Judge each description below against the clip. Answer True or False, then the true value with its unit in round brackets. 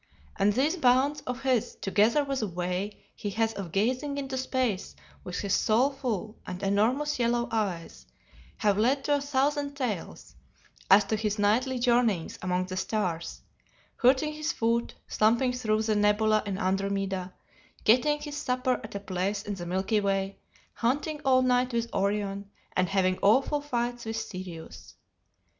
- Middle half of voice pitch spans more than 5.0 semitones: False (4.6 semitones)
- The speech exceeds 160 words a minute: False (155 wpm)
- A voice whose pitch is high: True (220 Hz)